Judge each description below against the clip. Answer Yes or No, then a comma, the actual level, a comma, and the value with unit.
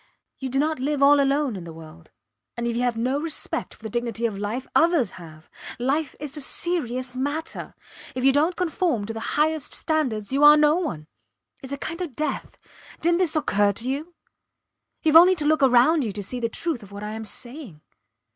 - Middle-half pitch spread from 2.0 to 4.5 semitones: No, wide, 5.4 semitones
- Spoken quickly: Yes, fast, 210 wpm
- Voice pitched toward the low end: No, very high, 265 Hz